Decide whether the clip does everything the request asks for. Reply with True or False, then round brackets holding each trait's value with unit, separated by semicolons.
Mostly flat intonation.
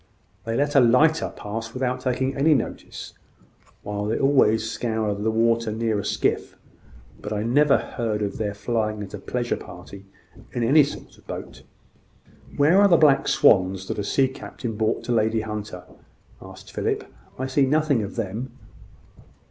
False (3.8 semitones)